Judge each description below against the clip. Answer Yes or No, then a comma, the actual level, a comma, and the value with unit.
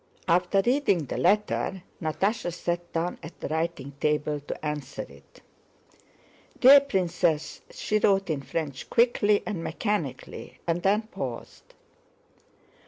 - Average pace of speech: No, slow, 120 wpm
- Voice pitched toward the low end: No, medium, 175 Hz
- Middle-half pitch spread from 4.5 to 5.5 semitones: Yes, average, 5.2 semitones